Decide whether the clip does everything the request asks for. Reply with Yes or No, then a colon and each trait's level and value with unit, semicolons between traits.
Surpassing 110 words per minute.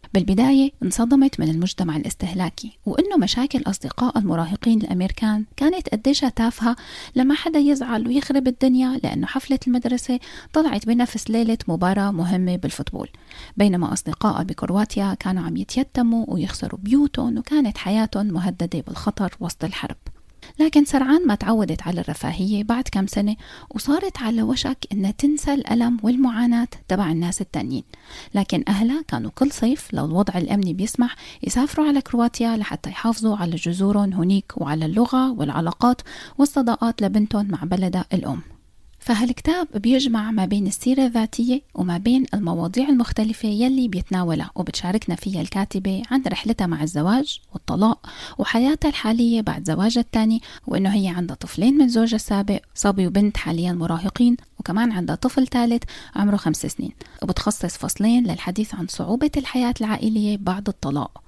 Yes: fast, 135 wpm